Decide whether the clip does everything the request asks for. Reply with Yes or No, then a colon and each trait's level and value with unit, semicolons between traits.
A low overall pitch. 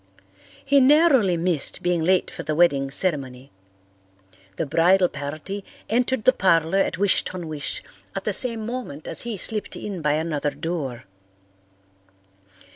No: medium, 175 Hz